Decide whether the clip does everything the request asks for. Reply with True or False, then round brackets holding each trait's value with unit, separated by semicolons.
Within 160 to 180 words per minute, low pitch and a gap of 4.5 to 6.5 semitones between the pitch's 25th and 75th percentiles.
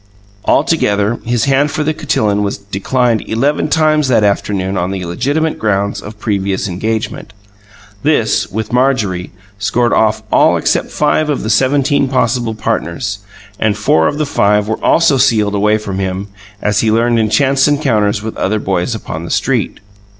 True (165 wpm; 110 Hz; 4.8 semitones)